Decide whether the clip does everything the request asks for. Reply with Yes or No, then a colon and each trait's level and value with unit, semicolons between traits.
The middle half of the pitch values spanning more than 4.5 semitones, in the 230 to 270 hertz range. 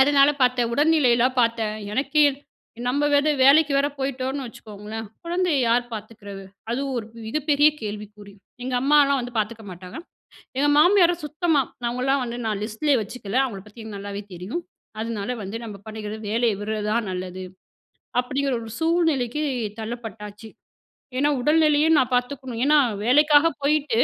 Yes: average, 4.9 semitones; high, 245 Hz